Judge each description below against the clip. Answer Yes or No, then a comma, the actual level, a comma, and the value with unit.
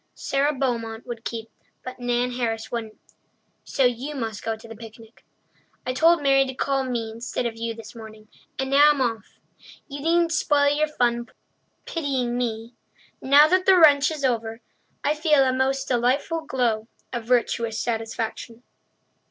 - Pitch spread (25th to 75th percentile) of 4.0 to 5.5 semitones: No, average, 3.6 semitones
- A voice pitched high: Yes, high, 245 Hz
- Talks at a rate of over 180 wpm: No, average, 160 wpm